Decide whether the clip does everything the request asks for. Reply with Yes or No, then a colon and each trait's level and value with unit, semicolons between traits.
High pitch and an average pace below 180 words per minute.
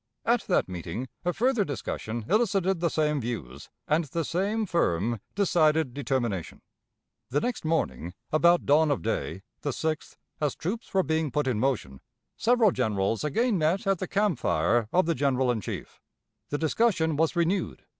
No: medium, 155 Hz; average, 165 wpm